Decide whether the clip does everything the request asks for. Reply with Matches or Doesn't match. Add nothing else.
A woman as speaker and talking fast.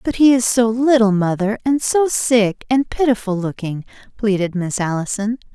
Doesn't match